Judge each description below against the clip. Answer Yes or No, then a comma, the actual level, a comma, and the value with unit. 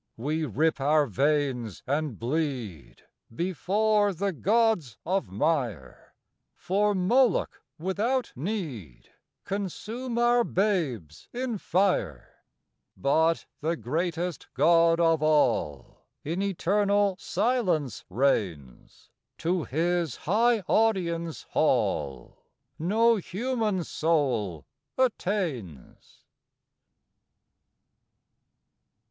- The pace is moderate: No, slow, 80 wpm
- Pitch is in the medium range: Yes, medium, 170 Hz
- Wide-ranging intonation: Yes, wide, 7.1 semitones